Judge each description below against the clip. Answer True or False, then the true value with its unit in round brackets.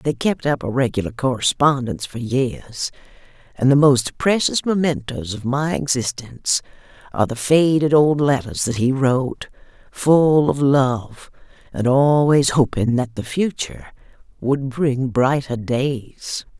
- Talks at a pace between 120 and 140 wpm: True (135 wpm)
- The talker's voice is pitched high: False (135 Hz)